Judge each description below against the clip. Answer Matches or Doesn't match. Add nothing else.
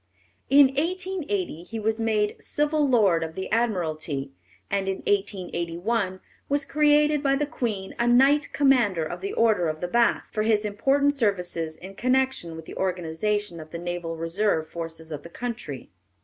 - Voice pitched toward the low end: Doesn't match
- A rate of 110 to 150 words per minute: Doesn't match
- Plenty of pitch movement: Matches